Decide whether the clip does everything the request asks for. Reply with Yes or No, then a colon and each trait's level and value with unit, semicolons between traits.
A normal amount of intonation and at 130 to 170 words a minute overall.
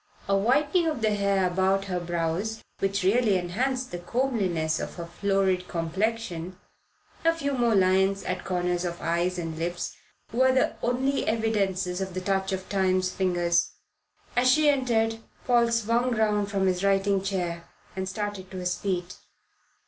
Yes: average, 4.0 semitones; average, 155 wpm